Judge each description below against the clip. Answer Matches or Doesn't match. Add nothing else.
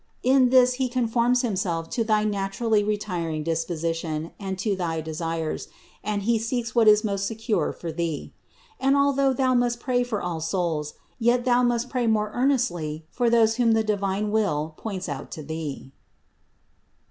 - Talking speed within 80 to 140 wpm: Doesn't match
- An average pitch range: Doesn't match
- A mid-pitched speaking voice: Doesn't match